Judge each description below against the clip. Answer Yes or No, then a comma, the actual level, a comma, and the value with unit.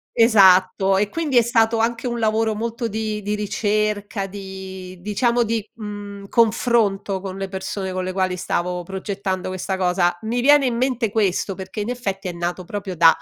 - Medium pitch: No, high, 205 Hz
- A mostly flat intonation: No, average, 3.1 semitones